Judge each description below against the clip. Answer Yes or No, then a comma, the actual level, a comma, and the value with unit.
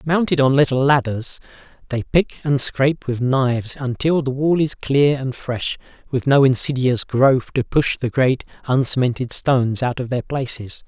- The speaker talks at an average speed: Yes, average, 170 wpm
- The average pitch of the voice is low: Yes, low, 130 Hz